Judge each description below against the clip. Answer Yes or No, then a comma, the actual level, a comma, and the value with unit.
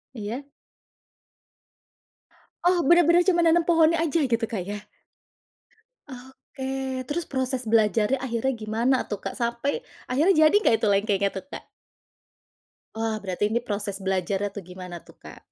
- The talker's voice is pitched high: Yes, high, 245 Hz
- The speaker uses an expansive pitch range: Yes, wide, 6.1 semitones